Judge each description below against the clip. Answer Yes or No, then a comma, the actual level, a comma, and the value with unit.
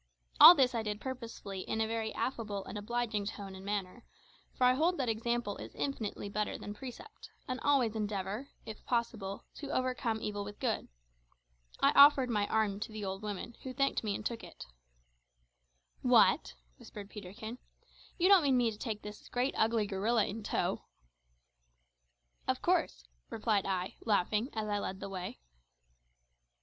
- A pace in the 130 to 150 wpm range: No, average, 165 wpm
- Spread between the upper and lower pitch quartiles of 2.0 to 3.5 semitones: Yes, average, 3.2 semitones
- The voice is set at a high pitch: Yes, high, 220 Hz